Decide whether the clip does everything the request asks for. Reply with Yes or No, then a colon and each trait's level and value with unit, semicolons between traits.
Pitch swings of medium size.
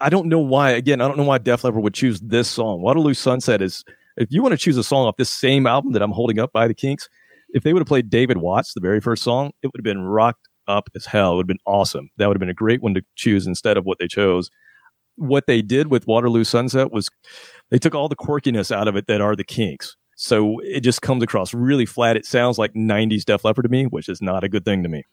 Yes: average, 4.1 semitones